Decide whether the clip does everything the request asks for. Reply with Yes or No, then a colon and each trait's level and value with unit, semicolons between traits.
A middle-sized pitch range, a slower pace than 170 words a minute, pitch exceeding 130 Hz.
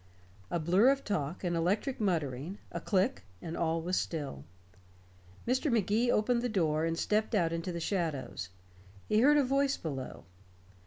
No: wide, 5.8 semitones; average, 160 wpm; medium, 185 Hz